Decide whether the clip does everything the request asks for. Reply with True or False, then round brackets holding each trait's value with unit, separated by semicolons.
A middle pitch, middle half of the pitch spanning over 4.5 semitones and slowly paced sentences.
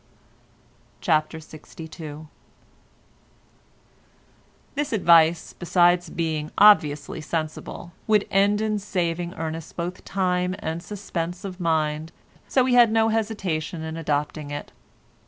False (170 Hz; 3.8 semitones; 105 wpm)